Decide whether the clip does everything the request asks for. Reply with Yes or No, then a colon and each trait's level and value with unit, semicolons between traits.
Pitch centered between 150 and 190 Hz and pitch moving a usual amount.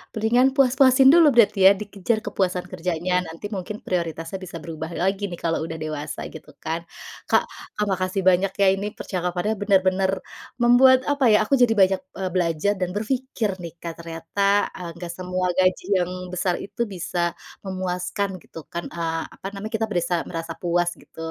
Yes: medium, 185 Hz; average, 3.2 semitones